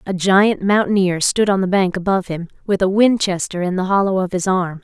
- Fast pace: Yes, fast, 225 wpm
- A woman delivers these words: Yes, female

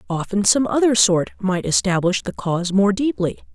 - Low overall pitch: No, high, 200 Hz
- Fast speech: No, average, 170 wpm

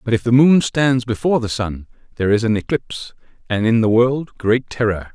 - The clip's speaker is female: No, male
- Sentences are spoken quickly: Yes, fast, 210 wpm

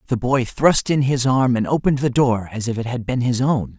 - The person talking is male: Yes, male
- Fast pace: Yes, fast, 270 wpm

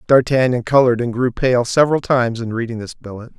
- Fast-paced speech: No, average, 195 wpm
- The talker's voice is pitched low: Yes, low, 120 Hz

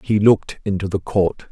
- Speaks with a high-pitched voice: No, low, 100 Hz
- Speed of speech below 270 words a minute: Yes, average, 200 wpm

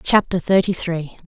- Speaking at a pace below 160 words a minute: Yes, average, 140 wpm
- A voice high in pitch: No, medium, 180 Hz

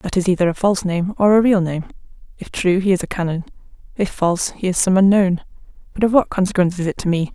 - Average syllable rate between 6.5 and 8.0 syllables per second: Yes, 6.6 syllables/s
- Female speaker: Yes, female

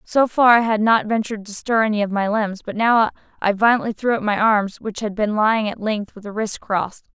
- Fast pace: Yes, fast, 245 wpm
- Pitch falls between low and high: No, high, 215 Hz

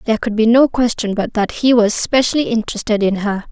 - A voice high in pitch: Yes, high, 230 Hz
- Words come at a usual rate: No, fast, 220 wpm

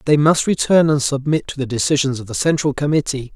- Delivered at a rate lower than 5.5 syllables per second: No, 5.9 syllables/s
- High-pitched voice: No, medium, 140 Hz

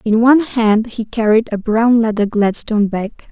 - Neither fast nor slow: Yes, average, 180 wpm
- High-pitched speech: Yes, high, 220 Hz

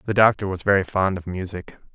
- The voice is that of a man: Yes, male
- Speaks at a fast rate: Yes, fast, 215 wpm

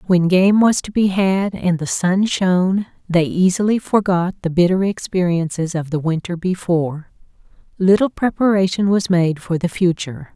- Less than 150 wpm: No, average, 155 wpm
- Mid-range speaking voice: Yes, medium, 180 Hz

